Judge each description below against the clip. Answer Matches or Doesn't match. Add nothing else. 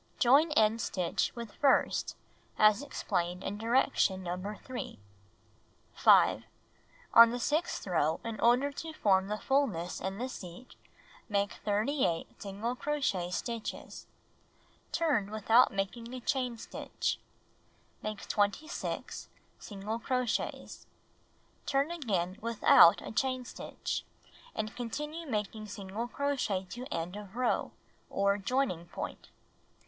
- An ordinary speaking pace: Doesn't match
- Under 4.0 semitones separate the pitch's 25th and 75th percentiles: Doesn't match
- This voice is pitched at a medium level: Doesn't match